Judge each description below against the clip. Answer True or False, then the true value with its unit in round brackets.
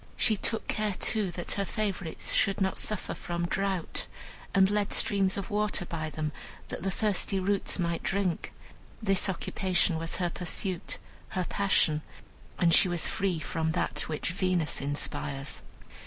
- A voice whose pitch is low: False (185 Hz)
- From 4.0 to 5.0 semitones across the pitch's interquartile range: False (3.0 semitones)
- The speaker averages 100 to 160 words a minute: True (155 wpm)